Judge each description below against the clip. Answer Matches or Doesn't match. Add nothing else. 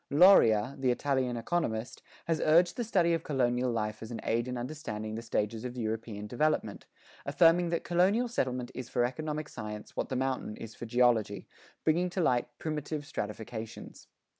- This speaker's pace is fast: Doesn't match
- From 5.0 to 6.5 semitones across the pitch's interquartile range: Matches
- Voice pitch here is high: Doesn't match